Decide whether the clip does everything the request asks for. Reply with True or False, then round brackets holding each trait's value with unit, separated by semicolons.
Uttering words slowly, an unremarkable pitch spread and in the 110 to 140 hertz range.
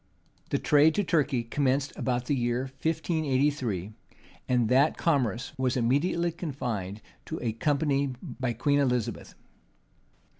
True (120 wpm; 3.4 semitones; 135 Hz)